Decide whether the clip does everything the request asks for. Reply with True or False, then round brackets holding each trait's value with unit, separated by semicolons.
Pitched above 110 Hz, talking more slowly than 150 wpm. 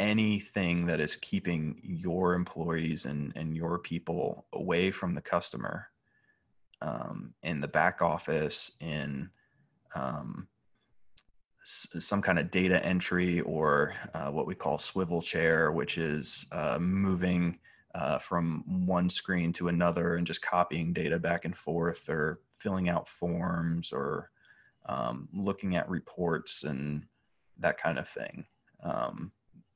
False (85 Hz; 135 wpm)